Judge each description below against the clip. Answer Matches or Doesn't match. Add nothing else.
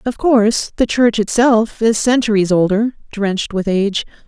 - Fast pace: Doesn't match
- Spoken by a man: Doesn't match